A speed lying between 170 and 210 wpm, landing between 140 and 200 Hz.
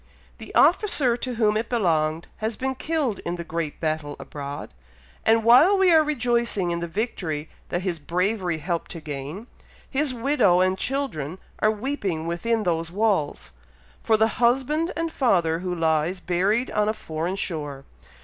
No: average, 160 wpm; high, 190 Hz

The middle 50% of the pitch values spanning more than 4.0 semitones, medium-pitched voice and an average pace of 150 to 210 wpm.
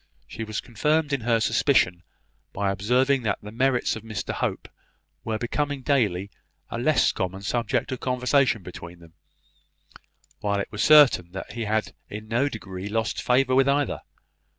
No: average, 4.6 semitones; low, 115 Hz; average, 160 wpm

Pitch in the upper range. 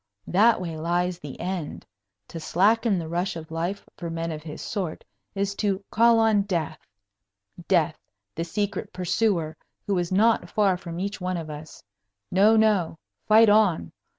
No: medium, 180 Hz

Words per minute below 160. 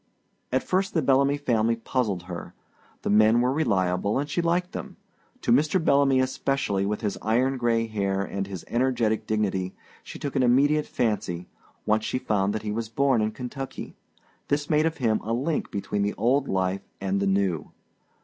No: average, 180 wpm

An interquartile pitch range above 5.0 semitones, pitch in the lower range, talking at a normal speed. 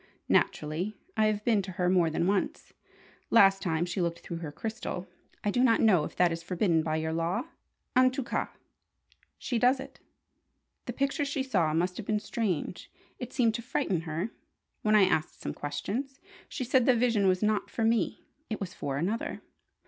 No: wide, 5.4 semitones; high, 200 Hz; average, 190 wpm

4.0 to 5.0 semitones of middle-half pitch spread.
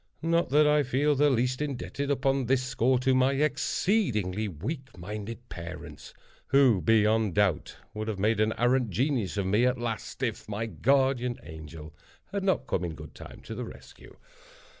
Yes: average, 4.7 semitones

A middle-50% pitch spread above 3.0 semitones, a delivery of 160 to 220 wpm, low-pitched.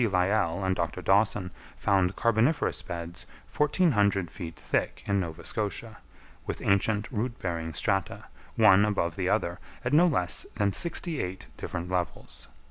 No: average, 3.8 semitones; average, 140 wpm; low, 100 Hz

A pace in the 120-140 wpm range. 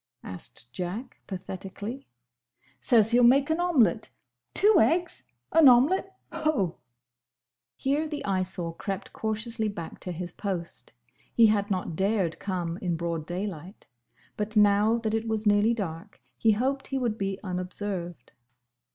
Yes: slow, 135 wpm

